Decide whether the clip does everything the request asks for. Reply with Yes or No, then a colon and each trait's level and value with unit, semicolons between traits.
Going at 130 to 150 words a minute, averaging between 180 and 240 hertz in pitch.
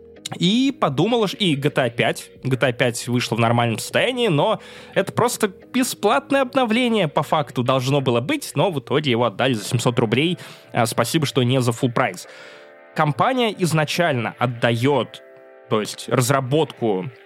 No: average, 145 wpm; low, 135 Hz